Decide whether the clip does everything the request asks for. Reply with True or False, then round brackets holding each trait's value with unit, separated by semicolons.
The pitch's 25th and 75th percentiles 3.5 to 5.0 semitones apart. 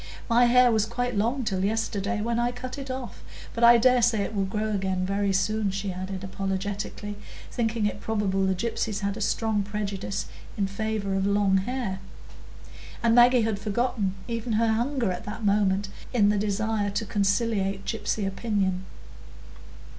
False (2.8 semitones)